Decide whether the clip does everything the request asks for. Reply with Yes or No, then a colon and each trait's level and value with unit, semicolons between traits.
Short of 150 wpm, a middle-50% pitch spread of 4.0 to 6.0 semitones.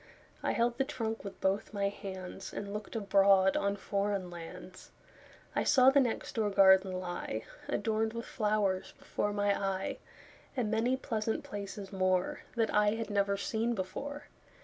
No: slow, 135 wpm; narrow, 2.6 semitones